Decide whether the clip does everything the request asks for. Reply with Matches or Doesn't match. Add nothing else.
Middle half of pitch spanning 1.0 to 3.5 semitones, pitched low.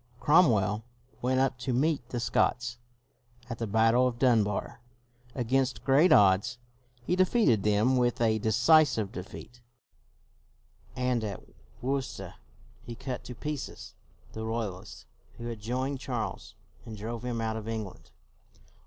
Matches